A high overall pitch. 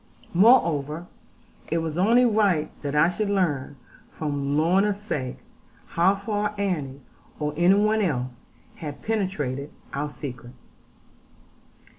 No: medium, 170 Hz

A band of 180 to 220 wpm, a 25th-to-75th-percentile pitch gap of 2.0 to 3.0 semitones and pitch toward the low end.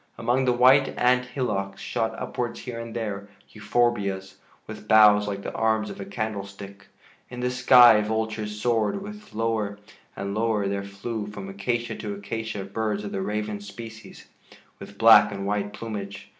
No: average, 155 wpm; narrow, 2.6 semitones; low, 105 Hz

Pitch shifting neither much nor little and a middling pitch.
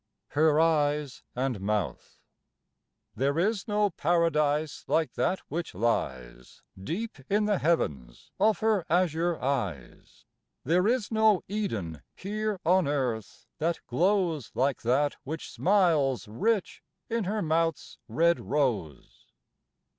No: wide, 6.6 semitones; medium, 160 Hz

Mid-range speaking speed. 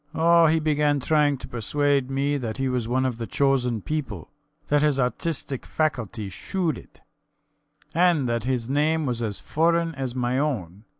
Yes: average, 170 wpm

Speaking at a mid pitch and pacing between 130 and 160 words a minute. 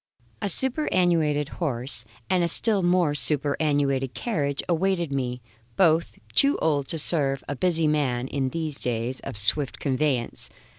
Yes: medium, 150 Hz; average, 140 wpm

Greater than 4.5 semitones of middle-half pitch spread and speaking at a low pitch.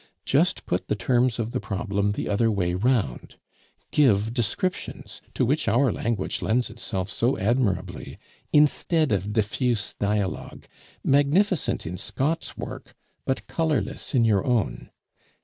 Yes: average, 5.0 semitones; low, 115 Hz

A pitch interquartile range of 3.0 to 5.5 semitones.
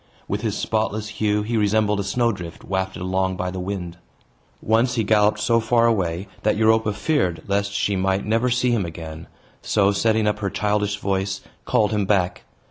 No: narrow, 2.5 semitones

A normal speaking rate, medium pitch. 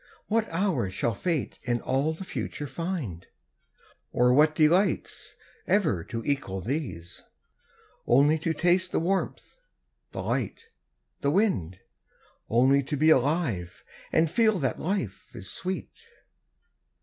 No: slow, 125 wpm; medium, 150 Hz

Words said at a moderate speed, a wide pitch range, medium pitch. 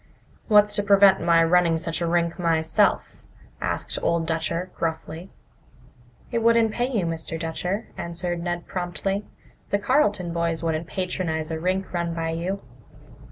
No: average, 145 wpm; average, 2.9 semitones; medium, 175 Hz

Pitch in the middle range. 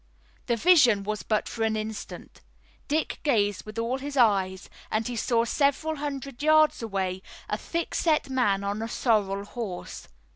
No: high, 230 Hz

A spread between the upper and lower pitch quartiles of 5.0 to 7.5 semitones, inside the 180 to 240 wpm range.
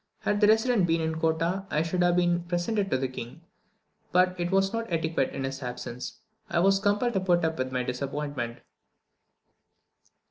Yes: average, 5.3 semitones; average, 185 wpm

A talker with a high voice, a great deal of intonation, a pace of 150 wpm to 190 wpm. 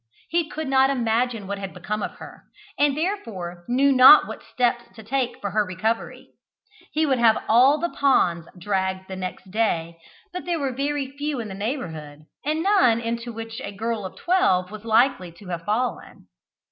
Yes: high, 230 Hz; wide, 6.1 semitones; average, 180 wpm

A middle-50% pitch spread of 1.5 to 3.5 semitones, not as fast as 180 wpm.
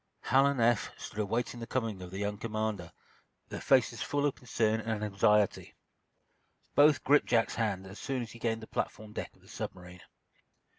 No: average, 2.8 semitones; average, 185 wpm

